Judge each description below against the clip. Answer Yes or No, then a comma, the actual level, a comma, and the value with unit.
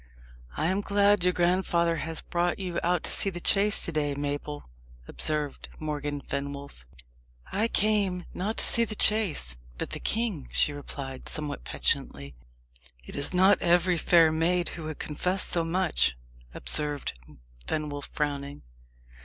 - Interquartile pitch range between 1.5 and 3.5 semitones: No, average, 4.2 semitones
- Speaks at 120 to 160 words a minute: Yes, average, 145 wpm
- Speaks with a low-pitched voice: No, medium, 165 Hz